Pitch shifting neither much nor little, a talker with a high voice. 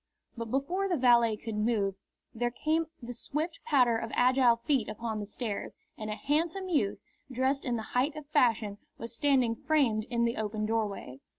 Yes: average, 4.3 semitones; high, 240 Hz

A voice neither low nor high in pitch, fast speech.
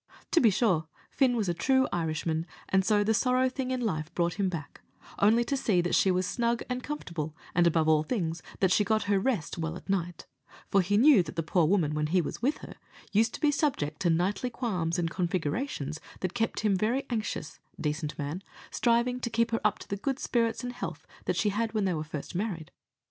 No: high, 195 Hz; fast, 225 wpm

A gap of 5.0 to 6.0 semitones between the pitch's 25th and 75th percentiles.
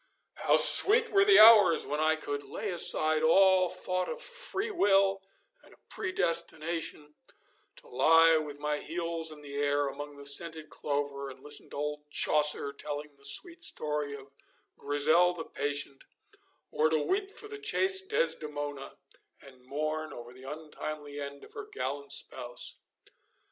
No: average, 4.3 semitones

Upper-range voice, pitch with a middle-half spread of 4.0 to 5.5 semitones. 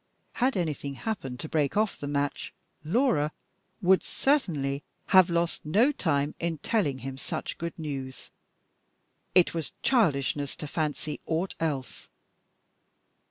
No: medium, 155 Hz; average, 4.7 semitones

